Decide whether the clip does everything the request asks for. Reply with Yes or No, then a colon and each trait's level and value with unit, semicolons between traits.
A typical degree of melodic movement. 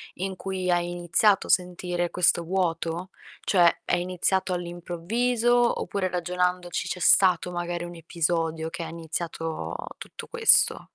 No: narrow, 1.5 semitones